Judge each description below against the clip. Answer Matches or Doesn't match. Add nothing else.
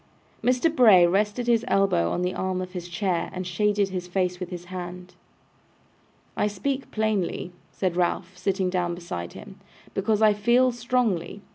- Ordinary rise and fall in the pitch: Matches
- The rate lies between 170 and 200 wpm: Doesn't match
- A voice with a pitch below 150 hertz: Doesn't match